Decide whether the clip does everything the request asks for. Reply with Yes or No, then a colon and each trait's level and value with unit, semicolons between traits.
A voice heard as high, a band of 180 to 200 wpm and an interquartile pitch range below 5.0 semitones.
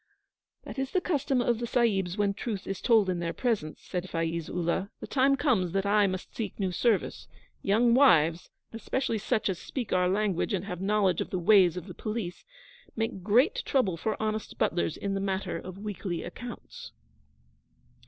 Yes: high, 200 Hz; average, 185 wpm; average, 4.4 semitones